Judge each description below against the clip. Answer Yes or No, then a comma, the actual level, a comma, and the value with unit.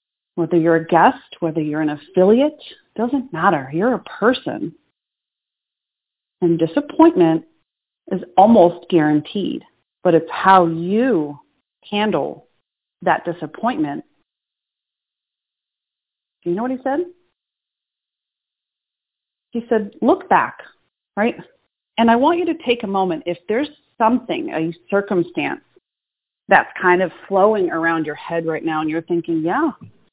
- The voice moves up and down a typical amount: No, wide, 7.1 semitones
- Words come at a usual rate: No, slow, 125 wpm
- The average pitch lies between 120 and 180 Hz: No, high, 190 Hz